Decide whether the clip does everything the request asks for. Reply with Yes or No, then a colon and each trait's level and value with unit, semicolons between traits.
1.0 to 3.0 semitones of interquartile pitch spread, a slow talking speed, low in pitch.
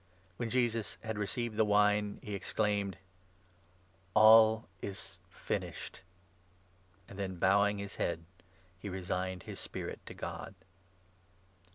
Yes: average, 2.7 semitones; slow, 115 wpm; low, 100 Hz